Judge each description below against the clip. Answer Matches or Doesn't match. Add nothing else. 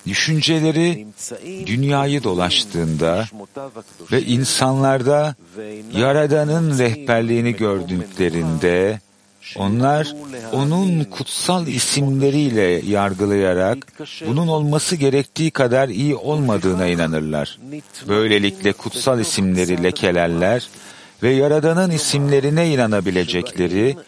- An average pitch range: Doesn't match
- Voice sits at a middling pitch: Doesn't match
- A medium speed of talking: Doesn't match